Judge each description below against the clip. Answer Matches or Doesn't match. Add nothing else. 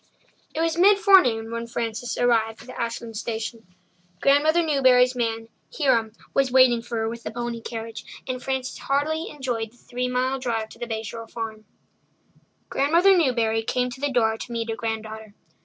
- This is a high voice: Matches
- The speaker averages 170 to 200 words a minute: Matches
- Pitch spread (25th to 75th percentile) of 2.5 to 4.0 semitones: Matches